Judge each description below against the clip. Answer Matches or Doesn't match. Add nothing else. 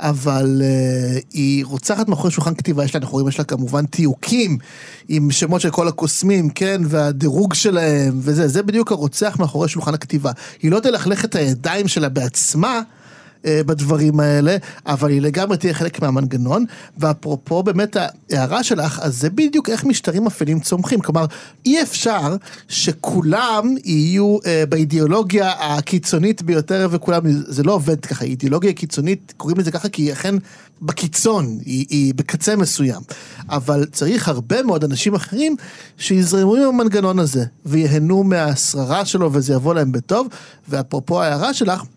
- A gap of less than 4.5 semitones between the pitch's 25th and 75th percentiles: Doesn't match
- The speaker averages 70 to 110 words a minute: Doesn't match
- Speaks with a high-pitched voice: Doesn't match